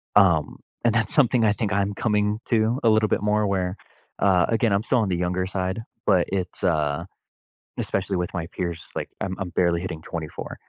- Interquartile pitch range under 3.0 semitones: No, average, 3.3 semitones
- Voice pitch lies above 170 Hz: No, very low, 95 Hz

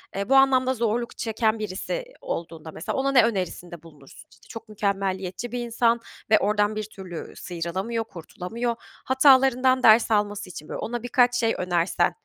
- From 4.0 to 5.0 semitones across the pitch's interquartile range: Yes, average, 4.5 semitones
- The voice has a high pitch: Yes, high, 215 Hz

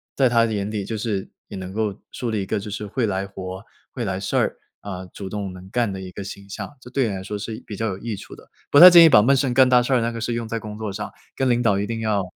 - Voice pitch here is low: Yes, low, 105 Hz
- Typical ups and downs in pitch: Yes, average, 3.2 semitones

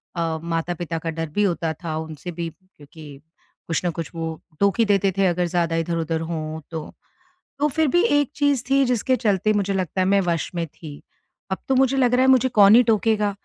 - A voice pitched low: No, medium, 180 Hz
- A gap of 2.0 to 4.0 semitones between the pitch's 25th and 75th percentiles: No, wide, 5.5 semitones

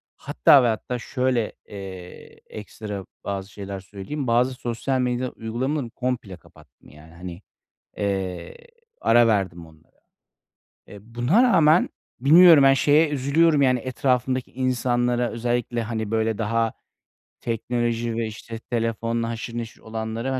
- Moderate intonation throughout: Yes, average, 3.3 semitones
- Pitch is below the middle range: Yes, low, 115 Hz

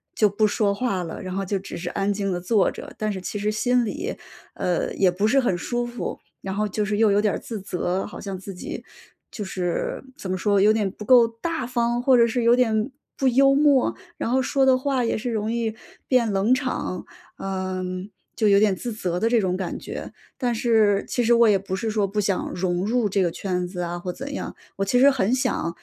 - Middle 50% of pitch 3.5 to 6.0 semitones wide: Yes, average, 4.0 semitones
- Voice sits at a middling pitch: No, high, 210 Hz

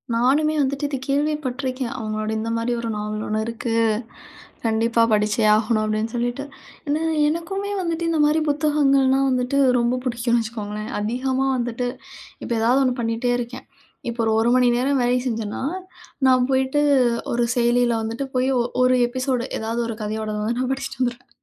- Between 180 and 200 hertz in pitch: No, high, 245 Hz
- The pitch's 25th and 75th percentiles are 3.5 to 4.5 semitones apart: No, average, 2.9 semitones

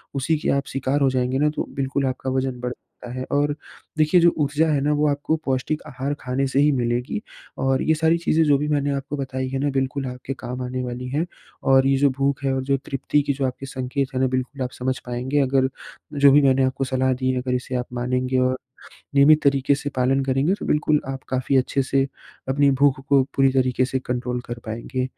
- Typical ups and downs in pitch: No, narrow, 1.7 semitones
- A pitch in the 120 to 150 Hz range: Yes, low, 135 Hz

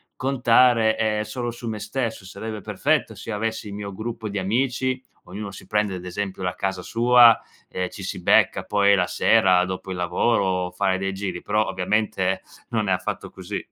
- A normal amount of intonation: Yes, average, 3.3 semitones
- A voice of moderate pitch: No, low, 105 Hz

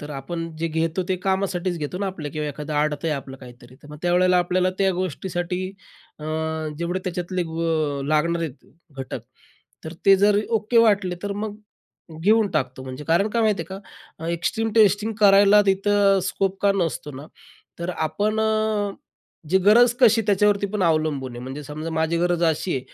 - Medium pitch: Yes, medium, 180 Hz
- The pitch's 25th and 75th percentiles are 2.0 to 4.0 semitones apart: No, average, 4.5 semitones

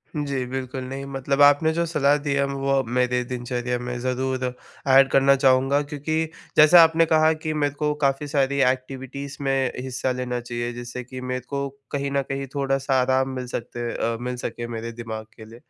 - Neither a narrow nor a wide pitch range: No, narrow, 1.9 semitones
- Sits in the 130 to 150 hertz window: Yes, low, 135 Hz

